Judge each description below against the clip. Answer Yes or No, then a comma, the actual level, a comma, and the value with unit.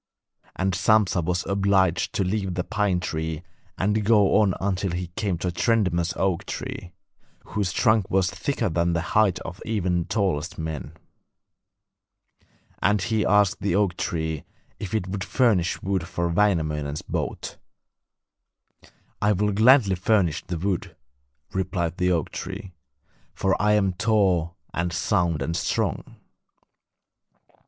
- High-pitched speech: No, very low, 95 Hz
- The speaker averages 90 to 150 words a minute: Yes, average, 140 wpm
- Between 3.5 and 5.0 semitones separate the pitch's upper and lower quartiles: No, average, 3.1 semitones